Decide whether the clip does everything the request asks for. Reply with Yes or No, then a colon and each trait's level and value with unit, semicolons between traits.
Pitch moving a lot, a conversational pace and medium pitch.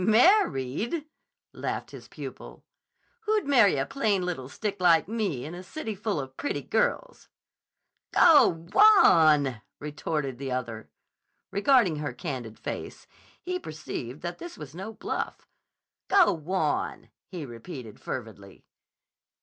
No: wide, 8.7 semitones; slow, 125 wpm; medium, 175 Hz